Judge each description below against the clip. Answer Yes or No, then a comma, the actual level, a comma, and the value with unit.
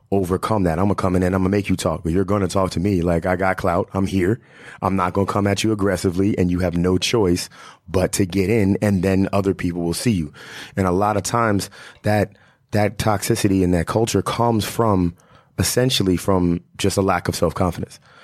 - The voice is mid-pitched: No, very low, 95 Hz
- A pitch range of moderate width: No, narrow, 2.2 semitones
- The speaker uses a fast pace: Yes, fast, 225 wpm